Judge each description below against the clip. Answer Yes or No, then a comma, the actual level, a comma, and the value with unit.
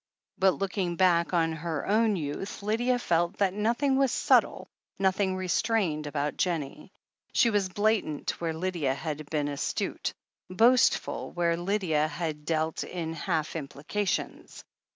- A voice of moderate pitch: Yes, medium, 175 Hz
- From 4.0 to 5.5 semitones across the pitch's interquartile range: Yes, average, 4.5 semitones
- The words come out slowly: Yes, slow, 130 wpm